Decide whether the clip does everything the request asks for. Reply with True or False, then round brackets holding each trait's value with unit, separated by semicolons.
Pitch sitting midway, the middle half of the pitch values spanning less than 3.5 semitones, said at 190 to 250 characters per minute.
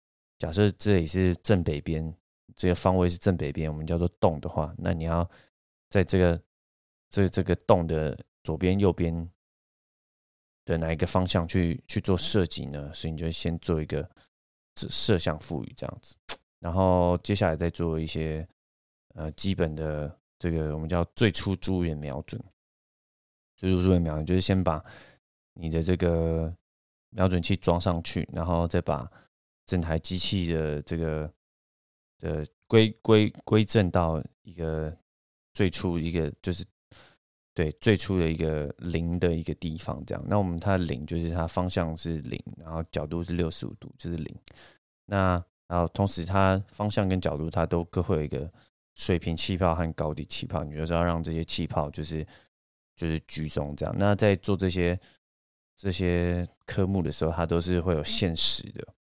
False (85 Hz; 2.9 semitones; 240 characters per minute)